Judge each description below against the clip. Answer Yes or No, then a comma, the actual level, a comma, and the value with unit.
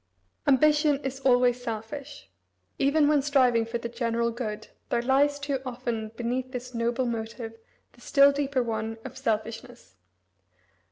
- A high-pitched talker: Yes, high, 245 Hz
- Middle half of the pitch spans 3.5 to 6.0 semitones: No, average, 2.9 semitones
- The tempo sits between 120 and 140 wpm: Yes, slow, 135 wpm